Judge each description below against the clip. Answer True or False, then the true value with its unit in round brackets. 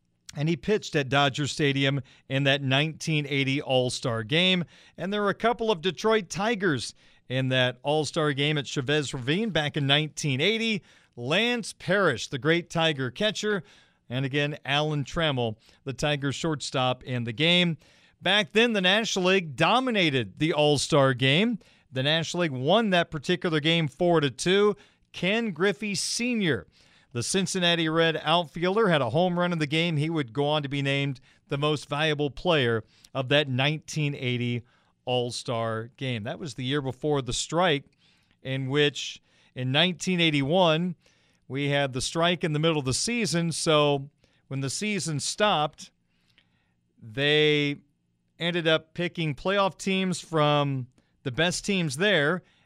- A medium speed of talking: True (155 wpm)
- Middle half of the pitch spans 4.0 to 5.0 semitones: True (4.5 semitones)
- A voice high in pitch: False (150 Hz)